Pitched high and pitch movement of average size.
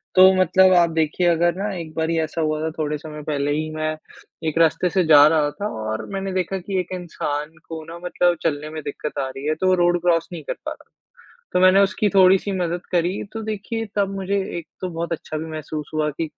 No: medium, 165 Hz; average, 3.0 semitones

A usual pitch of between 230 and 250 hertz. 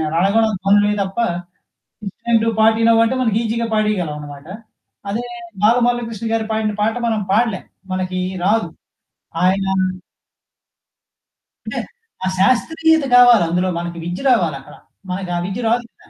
No: high, 215 Hz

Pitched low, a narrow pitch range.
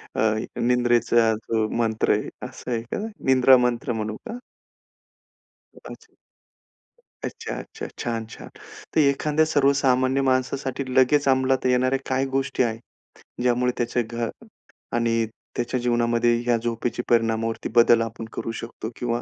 Yes: low, 120 Hz; narrow, 2.1 semitones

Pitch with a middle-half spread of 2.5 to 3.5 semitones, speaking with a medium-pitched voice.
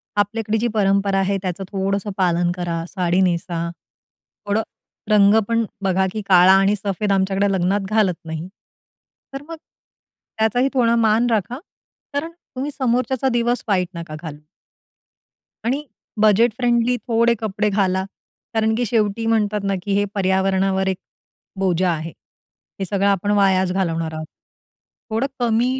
No: average, 3.1 semitones; high, 200 Hz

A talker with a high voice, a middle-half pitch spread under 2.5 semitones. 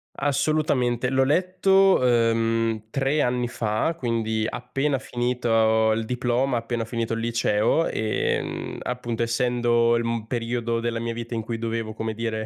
No: low, 115 Hz; narrow, 1.7 semitones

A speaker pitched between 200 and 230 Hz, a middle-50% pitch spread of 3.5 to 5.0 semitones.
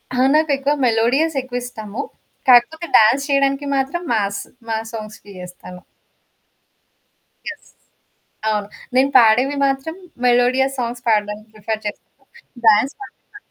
No: high, 245 Hz; average, 4.2 semitones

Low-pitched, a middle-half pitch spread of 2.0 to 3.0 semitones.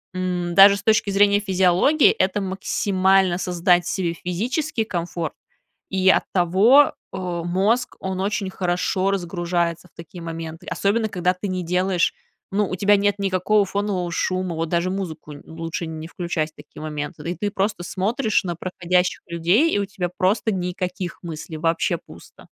No: medium, 185 Hz; narrow, 2.5 semitones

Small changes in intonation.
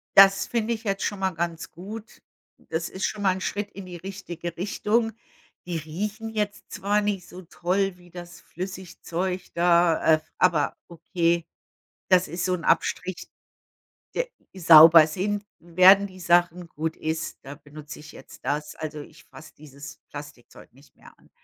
No: average, 3.2 semitones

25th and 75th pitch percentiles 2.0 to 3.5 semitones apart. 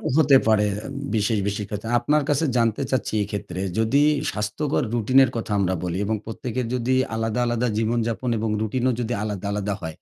Yes: average, 3.2 semitones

